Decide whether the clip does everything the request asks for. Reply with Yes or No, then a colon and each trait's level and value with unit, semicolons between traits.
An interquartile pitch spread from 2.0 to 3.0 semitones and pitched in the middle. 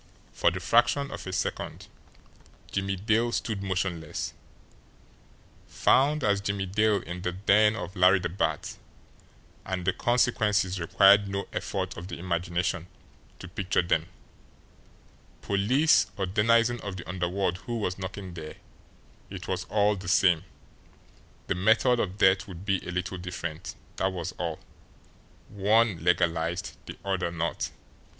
No: average, 2.7 semitones; very low, 95 Hz